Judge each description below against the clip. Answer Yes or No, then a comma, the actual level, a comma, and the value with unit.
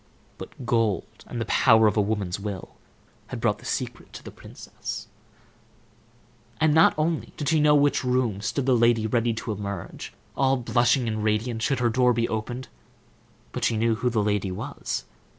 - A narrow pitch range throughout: No, average, 3.0 semitones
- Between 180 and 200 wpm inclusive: Yes, average, 185 wpm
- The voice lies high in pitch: No, low, 115 Hz